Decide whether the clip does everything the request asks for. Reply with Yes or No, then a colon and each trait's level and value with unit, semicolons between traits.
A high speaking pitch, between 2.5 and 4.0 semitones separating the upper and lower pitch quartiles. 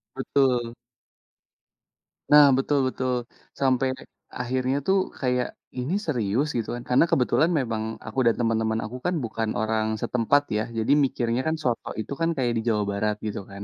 No: low, 125 Hz; average, 3.2 semitones